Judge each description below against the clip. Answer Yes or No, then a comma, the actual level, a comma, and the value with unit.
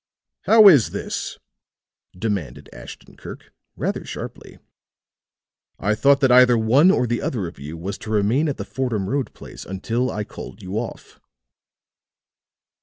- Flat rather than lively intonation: No, average, 4.7 semitones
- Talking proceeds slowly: No, average, 145 wpm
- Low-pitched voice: Yes, low, 115 Hz